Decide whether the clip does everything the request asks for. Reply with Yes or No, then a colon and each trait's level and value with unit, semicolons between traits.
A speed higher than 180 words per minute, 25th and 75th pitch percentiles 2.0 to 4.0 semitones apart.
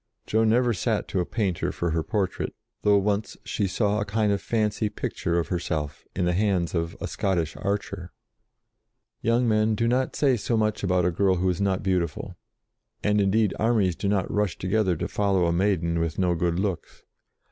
Yes: average, 190 wpm; average, 3.3 semitones